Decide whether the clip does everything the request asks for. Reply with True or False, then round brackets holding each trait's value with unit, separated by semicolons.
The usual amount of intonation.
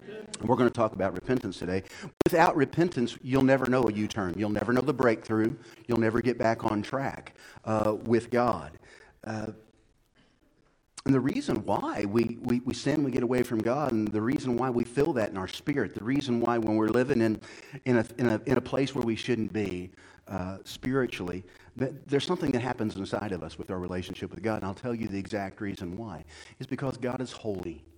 True (3.3 semitones)